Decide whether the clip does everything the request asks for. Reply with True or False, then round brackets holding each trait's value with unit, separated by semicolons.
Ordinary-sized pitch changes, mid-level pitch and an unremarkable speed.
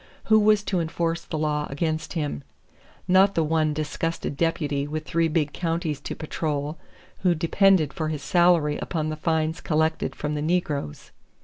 False (2.1 semitones; 160 Hz; 165 wpm)